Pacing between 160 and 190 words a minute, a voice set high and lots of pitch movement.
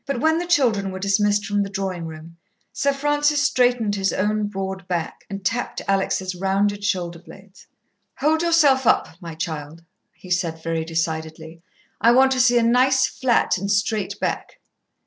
Yes: average, 165 wpm; high, 200 Hz; wide, 5.8 semitones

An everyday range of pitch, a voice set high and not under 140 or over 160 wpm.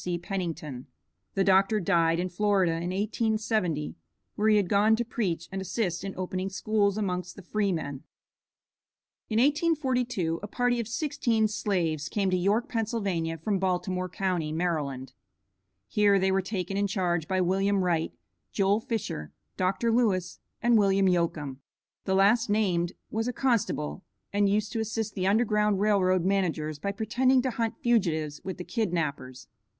Yes: average, 3.6 semitones; high, 195 Hz; average, 155 wpm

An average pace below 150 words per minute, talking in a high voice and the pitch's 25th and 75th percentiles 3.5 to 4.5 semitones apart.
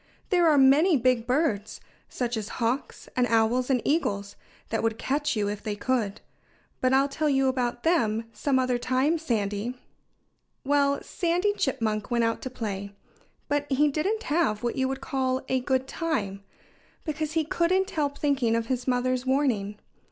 No: average, 165 wpm; very high, 260 Hz; average, 4.2 semitones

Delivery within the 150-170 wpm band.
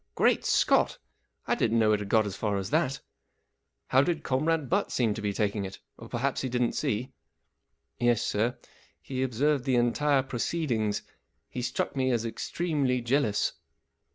No: average, 180 wpm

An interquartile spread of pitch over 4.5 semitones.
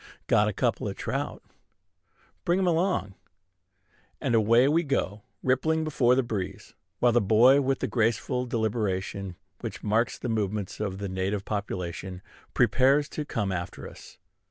Yes: average, 5.0 semitones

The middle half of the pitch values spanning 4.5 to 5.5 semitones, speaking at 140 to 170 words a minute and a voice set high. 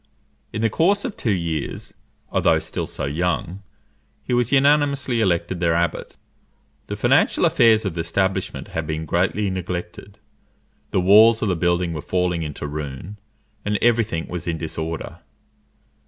No: average, 4.8 semitones; average, 155 wpm; very low, 90 Hz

